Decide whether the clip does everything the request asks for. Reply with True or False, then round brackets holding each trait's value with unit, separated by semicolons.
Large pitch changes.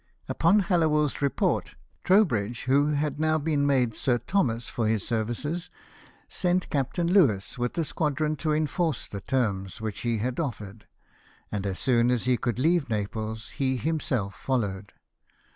True (5.7 semitones)